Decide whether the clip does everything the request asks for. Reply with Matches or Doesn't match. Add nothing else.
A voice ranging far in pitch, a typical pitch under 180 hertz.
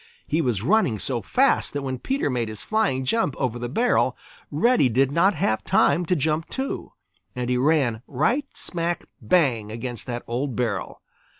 Matches